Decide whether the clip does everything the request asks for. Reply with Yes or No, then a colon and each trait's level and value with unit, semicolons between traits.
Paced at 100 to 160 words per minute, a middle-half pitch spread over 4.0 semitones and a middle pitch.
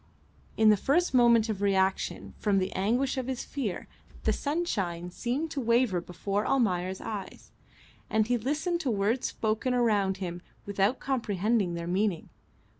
No: average, 150 wpm; average, 4.7 semitones; high, 215 Hz